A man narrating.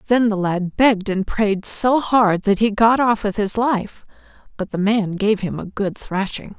No: female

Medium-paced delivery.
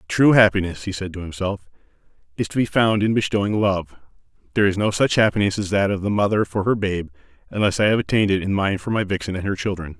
No: fast, 235 wpm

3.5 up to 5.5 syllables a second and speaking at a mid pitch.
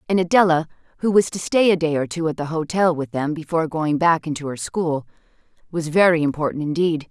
No: 5.9 syllables/s; medium, 160 Hz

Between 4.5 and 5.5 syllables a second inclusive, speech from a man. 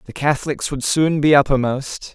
Yes: 5.0 syllables/s; male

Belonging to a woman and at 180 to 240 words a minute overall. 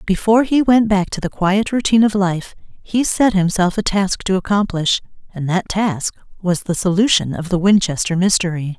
Yes: female; average, 185 wpm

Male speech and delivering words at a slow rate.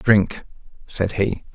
Yes: male; slow, 115 wpm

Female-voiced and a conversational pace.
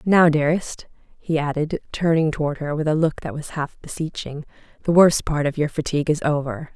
Yes: female; average, 195 wpm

